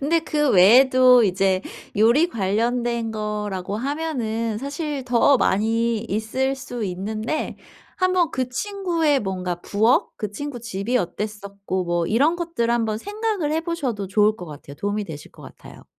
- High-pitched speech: Yes, high, 230 Hz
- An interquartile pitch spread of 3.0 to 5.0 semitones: No, wide, 5.6 semitones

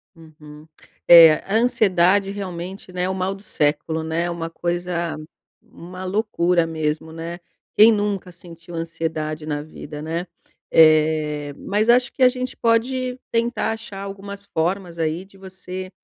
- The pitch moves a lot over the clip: No, average, 3.7 semitones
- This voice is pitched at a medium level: Yes, medium, 175 Hz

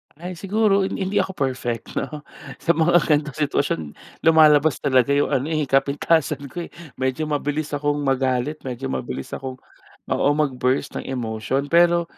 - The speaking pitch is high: No, medium, 145 Hz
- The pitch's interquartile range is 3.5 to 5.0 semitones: No, average, 3.1 semitones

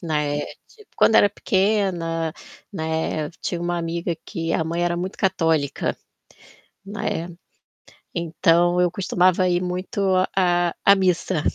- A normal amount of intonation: No, narrow, 2.1 semitones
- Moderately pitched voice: Yes, medium, 175 Hz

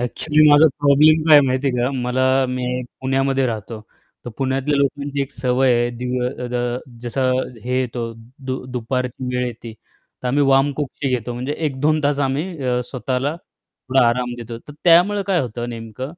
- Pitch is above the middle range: No, low, 130 Hz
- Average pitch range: No, narrow, 2.3 semitones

